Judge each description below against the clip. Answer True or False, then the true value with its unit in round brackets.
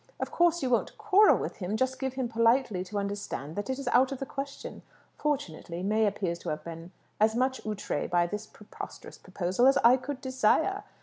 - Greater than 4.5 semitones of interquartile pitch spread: True (5.4 semitones)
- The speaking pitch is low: False (230 Hz)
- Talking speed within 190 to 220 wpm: True (200 wpm)